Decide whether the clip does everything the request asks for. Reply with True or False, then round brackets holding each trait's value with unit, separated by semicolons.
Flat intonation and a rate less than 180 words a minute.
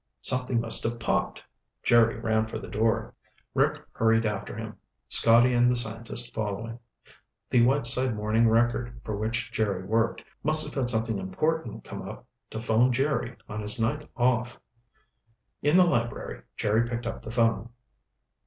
True (1.7 semitones; 155 wpm)